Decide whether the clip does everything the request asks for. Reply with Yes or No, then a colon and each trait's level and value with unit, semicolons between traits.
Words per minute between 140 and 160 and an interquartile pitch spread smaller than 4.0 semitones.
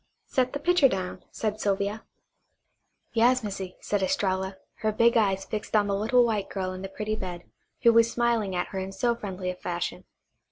No: average, 190 wpm; average, 3.3 semitones